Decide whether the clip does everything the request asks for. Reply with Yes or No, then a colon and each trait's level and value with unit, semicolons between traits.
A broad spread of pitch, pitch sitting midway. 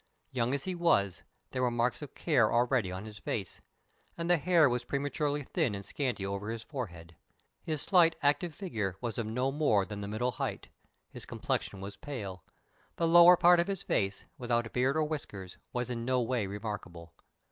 No: wide, 6.3 semitones; low, 125 Hz